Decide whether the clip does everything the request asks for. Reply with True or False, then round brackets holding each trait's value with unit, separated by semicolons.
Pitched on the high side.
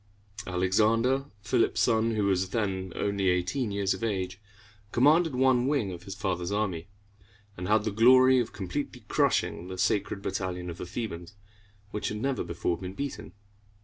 False (100 Hz)